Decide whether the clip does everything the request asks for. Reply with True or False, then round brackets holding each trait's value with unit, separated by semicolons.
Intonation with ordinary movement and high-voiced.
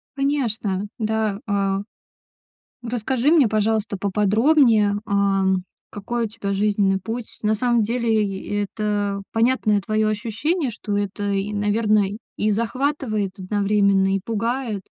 False (2.3 semitones; 210 Hz)